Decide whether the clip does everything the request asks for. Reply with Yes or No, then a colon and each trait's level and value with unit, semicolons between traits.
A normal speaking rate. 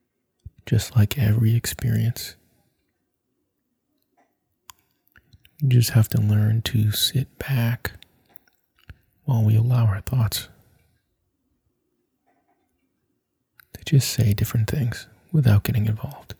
No: slow, 90 wpm